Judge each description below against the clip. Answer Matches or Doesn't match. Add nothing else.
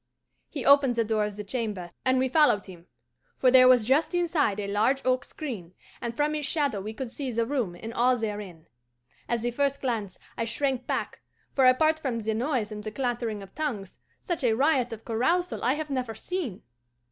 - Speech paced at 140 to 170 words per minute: Doesn't match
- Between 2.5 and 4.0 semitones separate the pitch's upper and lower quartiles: Doesn't match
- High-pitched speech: Matches